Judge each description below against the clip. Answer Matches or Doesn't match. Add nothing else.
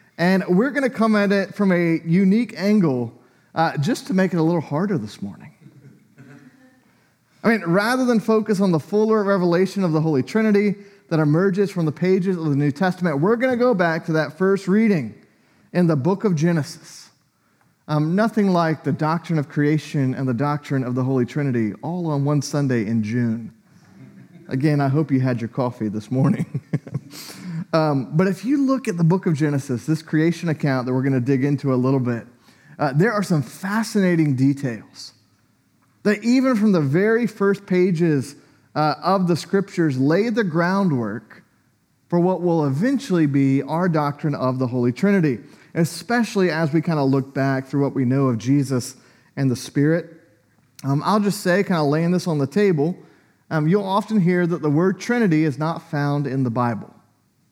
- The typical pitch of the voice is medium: Matches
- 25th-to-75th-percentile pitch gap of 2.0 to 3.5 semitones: Doesn't match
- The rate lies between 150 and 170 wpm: Doesn't match